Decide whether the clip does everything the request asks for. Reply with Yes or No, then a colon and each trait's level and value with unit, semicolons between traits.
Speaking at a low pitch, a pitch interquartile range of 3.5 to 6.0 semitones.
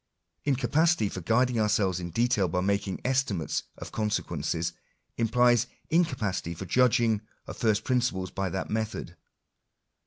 Yes: low, 105 Hz; average, 4.8 semitones